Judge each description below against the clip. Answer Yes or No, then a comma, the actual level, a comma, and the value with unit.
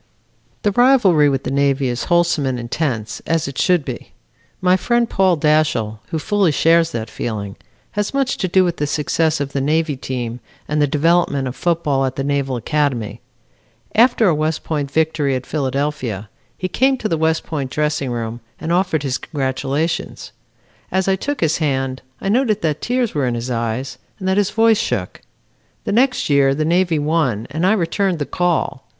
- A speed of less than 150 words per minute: No, average, 185 wpm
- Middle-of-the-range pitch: Yes, medium, 150 Hz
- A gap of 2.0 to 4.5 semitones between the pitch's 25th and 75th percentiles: No, average, 5.1 semitones